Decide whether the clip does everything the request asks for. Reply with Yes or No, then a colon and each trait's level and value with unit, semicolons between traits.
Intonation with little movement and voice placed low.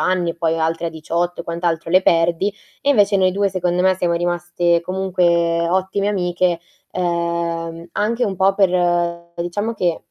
No: narrow, 1.8 semitones; medium, 175 Hz